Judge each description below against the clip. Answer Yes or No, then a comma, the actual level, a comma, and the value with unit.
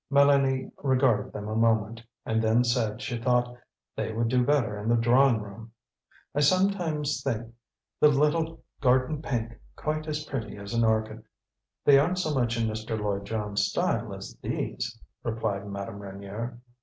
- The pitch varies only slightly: No, average, 4.1 semitones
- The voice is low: Yes, low, 115 Hz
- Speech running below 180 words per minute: Yes, average, 160 wpm